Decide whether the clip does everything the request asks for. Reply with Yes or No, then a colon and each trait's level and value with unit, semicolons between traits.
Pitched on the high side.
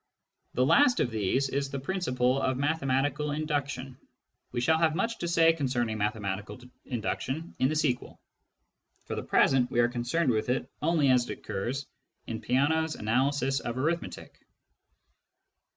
No: low, 135 Hz